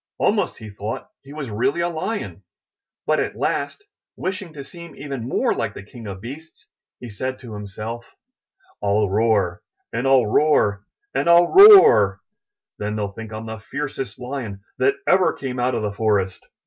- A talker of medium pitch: No, low, 115 Hz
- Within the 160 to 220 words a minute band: Yes, average, 175 wpm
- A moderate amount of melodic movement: No, wide, 5.9 semitones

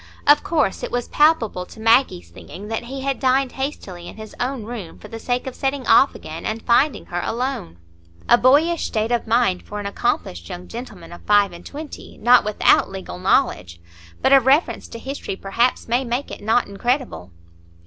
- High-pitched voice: Yes, high, 235 Hz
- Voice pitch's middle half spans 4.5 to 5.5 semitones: Yes, average, 5.1 semitones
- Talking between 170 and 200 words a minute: Yes, average, 190 wpm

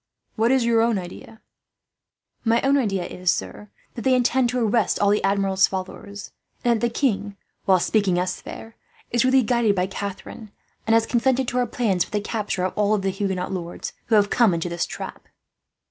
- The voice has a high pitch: Yes, high, 210 Hz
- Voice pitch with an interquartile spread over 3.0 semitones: Yes, average, 3.6 semitones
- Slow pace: No, average, 195 wpm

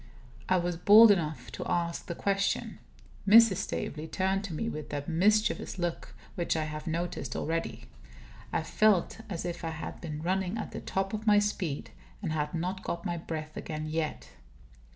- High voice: No, medium, 175 Hz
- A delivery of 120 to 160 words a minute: No, average, 175 wpm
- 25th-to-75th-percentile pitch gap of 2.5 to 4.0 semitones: Yes, average, 3.7 semitones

